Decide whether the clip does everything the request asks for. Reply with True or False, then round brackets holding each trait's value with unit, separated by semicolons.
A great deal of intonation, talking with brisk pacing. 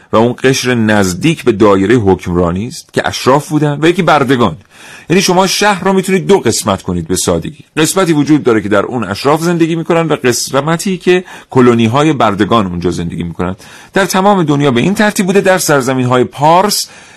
True (8.6 semitones; 185 wpm)